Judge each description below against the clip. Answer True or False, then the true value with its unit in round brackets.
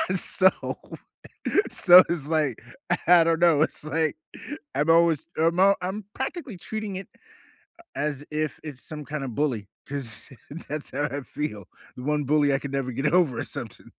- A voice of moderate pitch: True (150 Hz)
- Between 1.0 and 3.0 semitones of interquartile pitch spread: False (3.7 semitones)